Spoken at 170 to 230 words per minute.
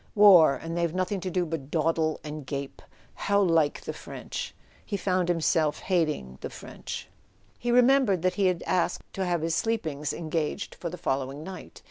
Yes: average, 175 wpm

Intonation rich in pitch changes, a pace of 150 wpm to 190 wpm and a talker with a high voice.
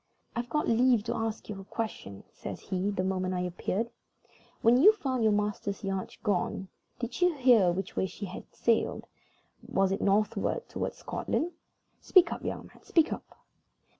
No: average, 4.1 semitones; average, 170 wpm; high, 210 Hz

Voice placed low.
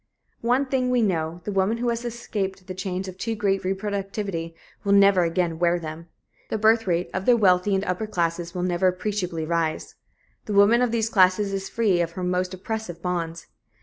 No: high, 190 Hz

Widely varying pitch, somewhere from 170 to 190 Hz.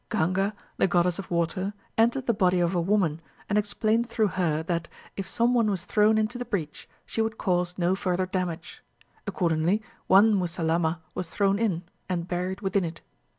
No: average, 3.4 semitones; medium, 185 Hz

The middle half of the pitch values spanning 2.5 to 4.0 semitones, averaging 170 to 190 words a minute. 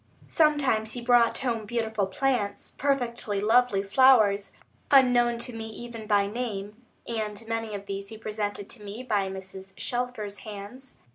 No: average, 3.2 semitones; average, 145 wpm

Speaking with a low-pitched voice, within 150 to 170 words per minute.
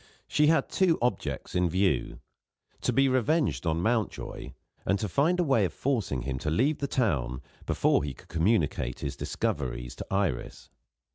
Yes: low, 100 Hz; average, 165 wpm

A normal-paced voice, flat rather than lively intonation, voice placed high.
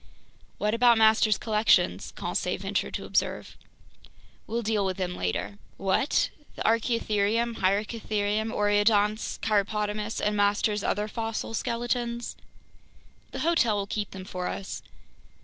No: slow, 120 wpm; narrow, 1.9 semitones; high, 215 Hz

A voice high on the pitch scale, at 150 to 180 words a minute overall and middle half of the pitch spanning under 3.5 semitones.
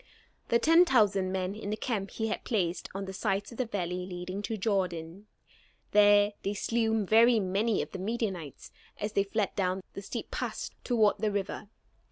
No: high, 205 Hz; average, 190 wpm; narrow, 2.6 semitones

